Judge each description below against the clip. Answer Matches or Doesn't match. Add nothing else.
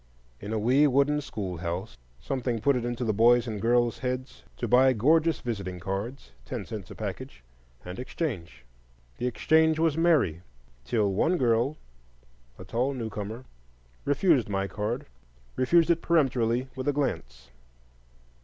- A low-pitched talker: Matches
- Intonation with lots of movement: Matches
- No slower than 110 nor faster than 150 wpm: Matches